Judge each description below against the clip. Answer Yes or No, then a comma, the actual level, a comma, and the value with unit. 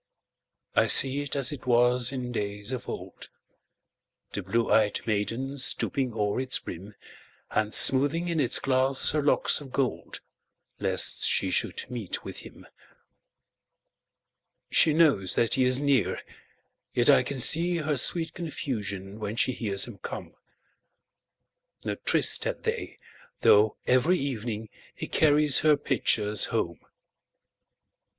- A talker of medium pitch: No, low, 125 Hz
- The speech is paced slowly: Yes, slow, 120 wpm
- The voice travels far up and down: No, average, 4.8 semitones